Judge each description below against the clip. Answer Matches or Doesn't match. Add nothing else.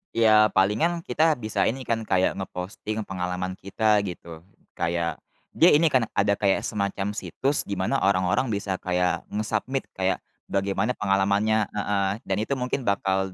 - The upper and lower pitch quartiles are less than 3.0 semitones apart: Matches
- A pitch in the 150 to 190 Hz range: Doesn't match